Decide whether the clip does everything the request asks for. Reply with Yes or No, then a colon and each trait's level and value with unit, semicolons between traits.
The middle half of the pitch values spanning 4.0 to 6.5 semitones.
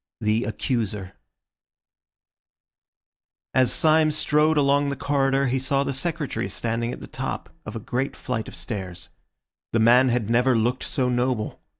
No: average, 3.5 semitones